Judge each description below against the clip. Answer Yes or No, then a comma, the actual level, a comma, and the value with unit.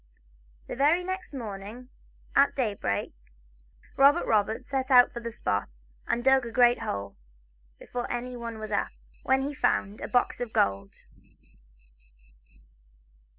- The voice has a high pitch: Yes, high, 240 Hz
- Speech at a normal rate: No, slow, 130 wpm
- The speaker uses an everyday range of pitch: Yes, average, 4.2 semitones